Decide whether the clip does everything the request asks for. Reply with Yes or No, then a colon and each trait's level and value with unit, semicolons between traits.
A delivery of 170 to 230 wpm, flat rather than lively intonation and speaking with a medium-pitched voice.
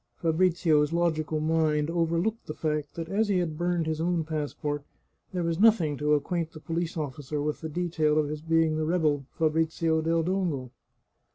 Yes: average, 175 wpm; narrow, 2.0 semitones; medium, 160 Hz